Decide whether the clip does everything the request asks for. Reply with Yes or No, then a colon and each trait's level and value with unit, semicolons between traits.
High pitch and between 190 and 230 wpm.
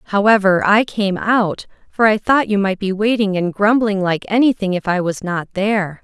Yes: high, 205 Hz; average, 200 wpm